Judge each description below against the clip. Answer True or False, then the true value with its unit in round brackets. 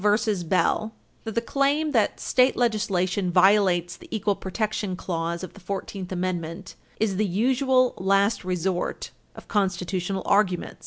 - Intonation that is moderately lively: True (3.0 semitones)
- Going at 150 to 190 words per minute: False (140 wpm)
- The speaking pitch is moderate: False (195 Hz)